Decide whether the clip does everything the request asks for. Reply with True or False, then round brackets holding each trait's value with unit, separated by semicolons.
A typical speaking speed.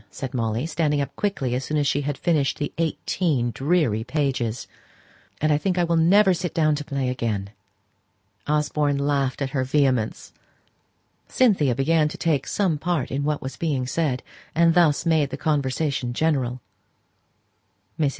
True (160 wpm)